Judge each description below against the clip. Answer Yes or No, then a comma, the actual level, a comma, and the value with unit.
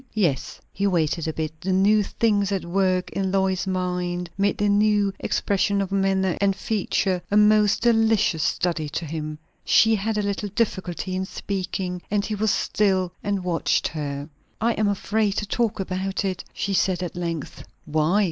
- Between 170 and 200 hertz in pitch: Yes, high, 190 Hz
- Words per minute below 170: No, average, 175 wpm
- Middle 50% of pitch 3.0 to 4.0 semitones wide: No, narrow, 2.4 semitones